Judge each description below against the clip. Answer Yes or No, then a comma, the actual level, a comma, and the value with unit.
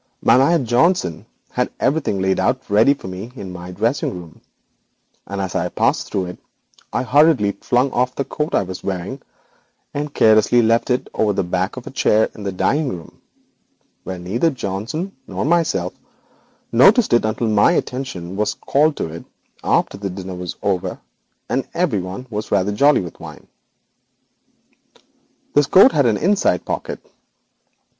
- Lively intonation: Yes, wide, 6.6 semitones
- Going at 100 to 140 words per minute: No, average, 165 wpm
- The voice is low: Yes, low, 110 Hz